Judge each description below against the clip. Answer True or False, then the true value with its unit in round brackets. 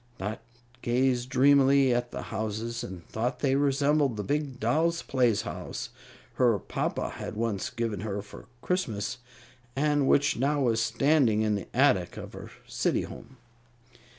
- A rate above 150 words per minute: False (145 wpm)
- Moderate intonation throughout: True (4.2 semitones)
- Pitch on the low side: True (125 Hz)